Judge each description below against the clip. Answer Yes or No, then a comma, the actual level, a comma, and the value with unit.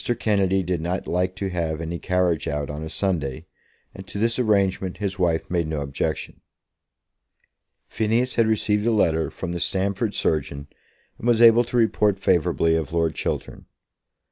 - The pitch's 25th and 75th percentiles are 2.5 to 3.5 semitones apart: No, average, 4.3 semitones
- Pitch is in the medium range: No, very low, 90 Hz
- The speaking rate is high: No, average, 165 wpm